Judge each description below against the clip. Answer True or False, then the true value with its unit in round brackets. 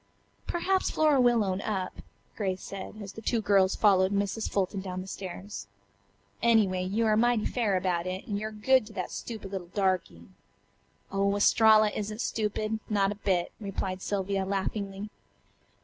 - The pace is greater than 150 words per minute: True (160 wpm)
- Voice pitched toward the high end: True (200 Hz)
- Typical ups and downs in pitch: False (2.3 semitones)